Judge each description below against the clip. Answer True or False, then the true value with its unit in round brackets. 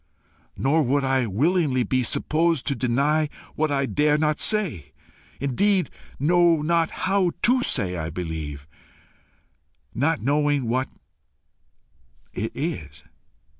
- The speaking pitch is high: False (145 Hz)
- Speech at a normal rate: False (115 wpm)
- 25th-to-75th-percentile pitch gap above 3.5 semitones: True (5.5 semitones)